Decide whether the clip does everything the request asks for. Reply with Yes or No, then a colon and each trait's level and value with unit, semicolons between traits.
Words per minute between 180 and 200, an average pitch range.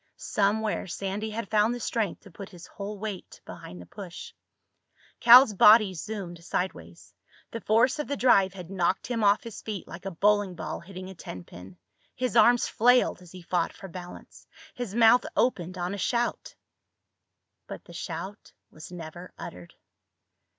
No: average, 165 wpm; average, 3.8 semitones